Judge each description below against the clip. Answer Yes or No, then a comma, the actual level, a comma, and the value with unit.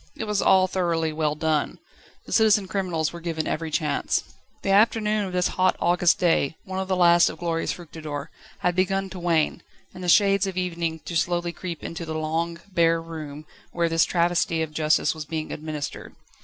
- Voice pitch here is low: No, medium, 170 Hz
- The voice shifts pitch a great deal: No, narrow, 2.5 semitones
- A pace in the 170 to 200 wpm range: Yes, average, 190 wpm